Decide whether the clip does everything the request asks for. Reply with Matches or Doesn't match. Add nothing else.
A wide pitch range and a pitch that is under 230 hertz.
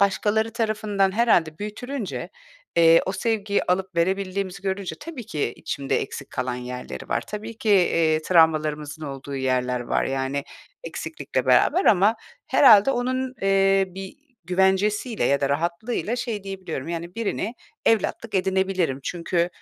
Doesn't match